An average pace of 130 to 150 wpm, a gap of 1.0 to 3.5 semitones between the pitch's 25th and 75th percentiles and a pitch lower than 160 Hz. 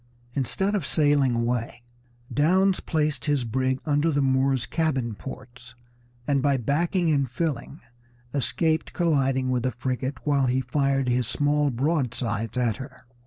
Yes: average, 140 wpm; average, 2.9 semitones; low, 135 Hz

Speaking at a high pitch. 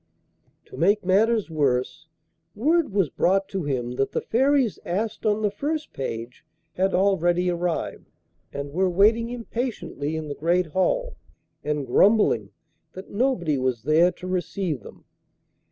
No: medium, 180 Hz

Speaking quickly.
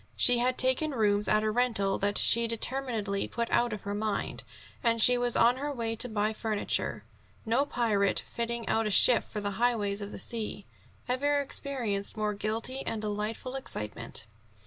No: average, 175 wpm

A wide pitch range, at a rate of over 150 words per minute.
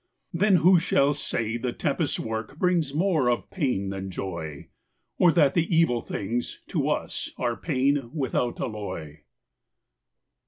No: wide, 6.7 semitones; slow, 135 wpm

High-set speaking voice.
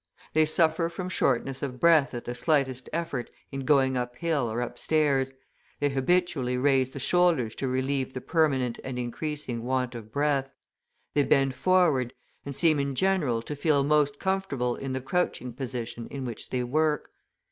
No: low, 135 Hz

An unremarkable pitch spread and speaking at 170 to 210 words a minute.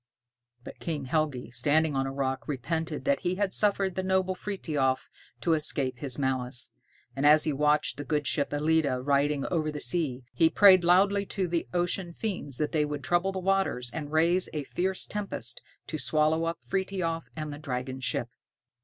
Yes: average, 4.3 semitones; average, 180 wpm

